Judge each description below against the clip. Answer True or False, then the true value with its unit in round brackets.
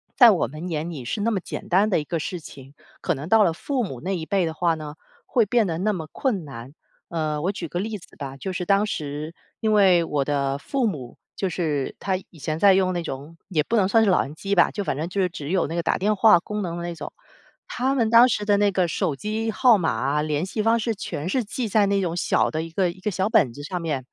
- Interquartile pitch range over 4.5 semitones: True (5.0 semitones)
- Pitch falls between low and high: True (180 Hz)